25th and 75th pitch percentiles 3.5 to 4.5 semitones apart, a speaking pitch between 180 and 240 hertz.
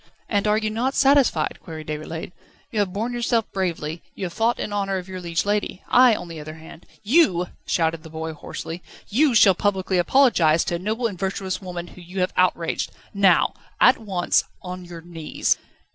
Yes: average, 4.1 semitones; medium, 185 Hz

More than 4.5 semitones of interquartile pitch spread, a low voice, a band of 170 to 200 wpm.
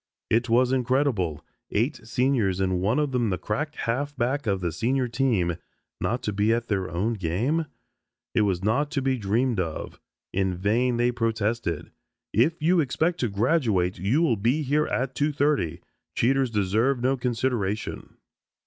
No: average, 5.1 semitones; low, 120 Hz; average, 160 wpm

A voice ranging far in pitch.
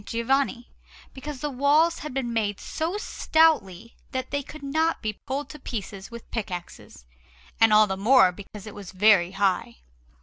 Yes: wide, 5.9 semitones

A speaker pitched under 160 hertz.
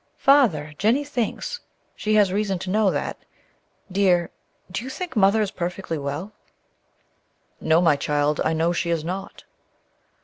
No: high, 190 Hz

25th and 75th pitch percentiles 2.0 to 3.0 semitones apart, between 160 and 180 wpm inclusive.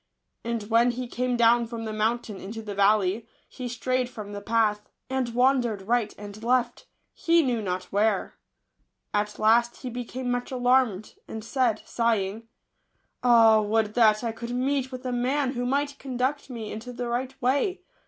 Yes: narrow, 2.6 semitones; average, 175 wpm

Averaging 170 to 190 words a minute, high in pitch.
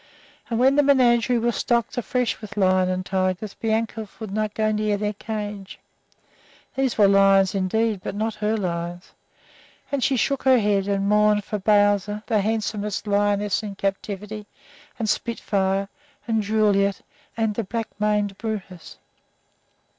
No: average, 145 wpm; high, 210 Hz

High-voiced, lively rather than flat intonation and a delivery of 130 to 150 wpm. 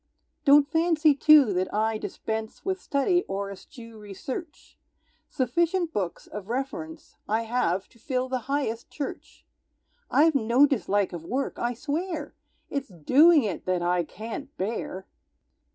Yes: very high, 250 Hz; wide, 6.1 semitones; slow, 135 wpm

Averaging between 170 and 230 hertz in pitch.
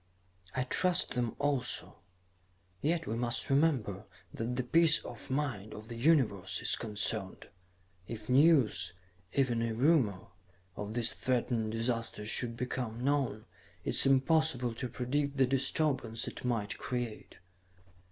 No: low, 125 Hz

